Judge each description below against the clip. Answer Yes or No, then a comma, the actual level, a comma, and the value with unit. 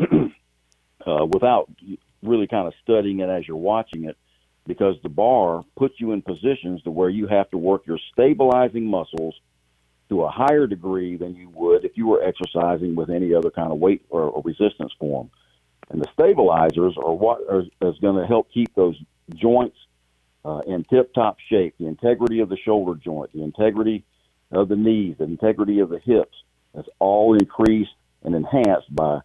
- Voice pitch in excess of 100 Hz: No, very low, 95 Hz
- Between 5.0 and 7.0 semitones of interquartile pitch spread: Yes, wide, 5.6 semitones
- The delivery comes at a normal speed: Yes, average, 180 wpm